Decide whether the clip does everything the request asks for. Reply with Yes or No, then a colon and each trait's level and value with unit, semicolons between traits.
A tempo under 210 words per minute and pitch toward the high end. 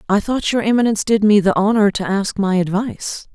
No: fast, 215 wpm; high, 210 Hz